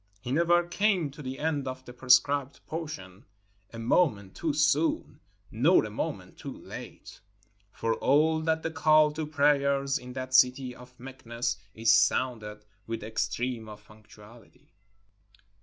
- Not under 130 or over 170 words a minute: Yes, average, 145 wpm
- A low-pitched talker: Yes, low, 130 Hz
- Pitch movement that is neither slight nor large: Yes, average, 4.8 semitones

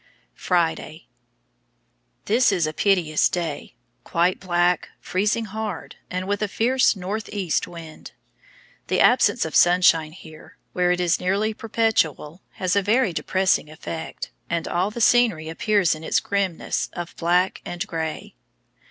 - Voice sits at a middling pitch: Yes, medium, 180 Hz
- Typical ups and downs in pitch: Yes, average, 3.5 semitones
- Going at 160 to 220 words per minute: No, average, 140 wpm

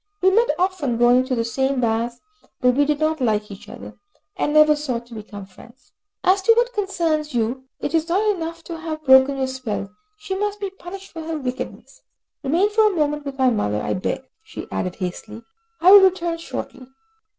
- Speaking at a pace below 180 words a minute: No, average, 200 wpm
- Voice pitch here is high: Yes, very high, 295 Hz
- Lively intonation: Yes, wide, 6.7 semitones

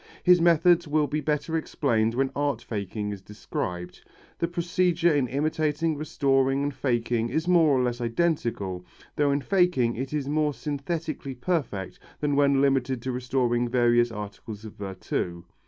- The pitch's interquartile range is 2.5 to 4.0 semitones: No, average, 4.6 semitones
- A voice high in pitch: No, low, 135 Hz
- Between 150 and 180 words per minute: Yes, average, 155 wpm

